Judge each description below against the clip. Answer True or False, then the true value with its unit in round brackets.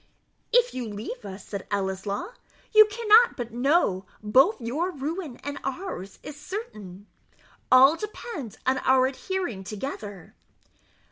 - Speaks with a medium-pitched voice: False (265 Hz)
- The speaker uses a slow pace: True (125 wpm)